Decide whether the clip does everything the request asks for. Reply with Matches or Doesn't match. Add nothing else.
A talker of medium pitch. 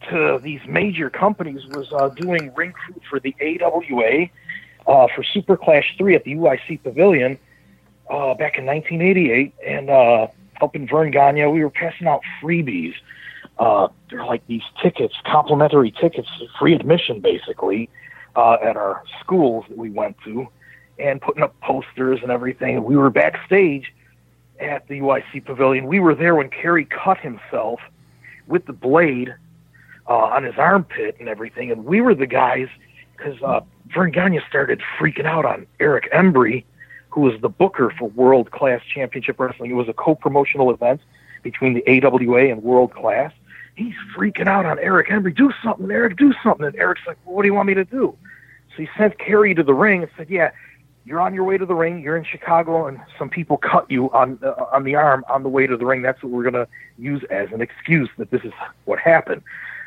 Matches